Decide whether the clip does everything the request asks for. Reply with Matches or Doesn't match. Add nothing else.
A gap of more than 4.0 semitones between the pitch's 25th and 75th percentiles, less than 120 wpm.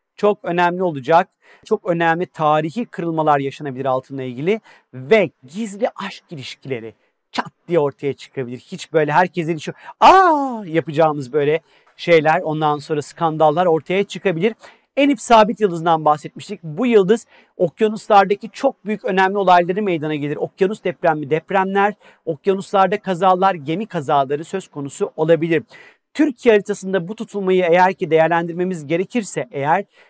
Doesn't match